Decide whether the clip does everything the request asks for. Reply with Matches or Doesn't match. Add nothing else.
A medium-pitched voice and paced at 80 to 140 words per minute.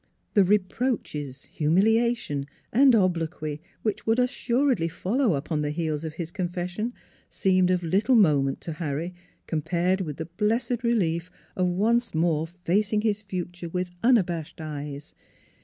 Matches